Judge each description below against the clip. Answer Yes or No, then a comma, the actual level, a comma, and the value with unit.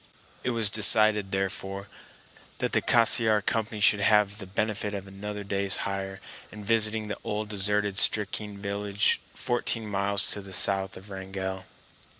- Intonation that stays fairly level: Yes, narrow, 1.5 semitones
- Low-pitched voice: Yes, low, 100 Hz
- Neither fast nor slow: Yes, average, 150 wpm